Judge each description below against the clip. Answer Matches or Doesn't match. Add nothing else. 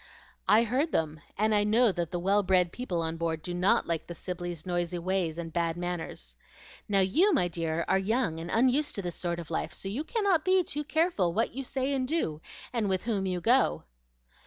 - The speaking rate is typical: Doesn't match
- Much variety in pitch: Matches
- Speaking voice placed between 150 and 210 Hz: Matches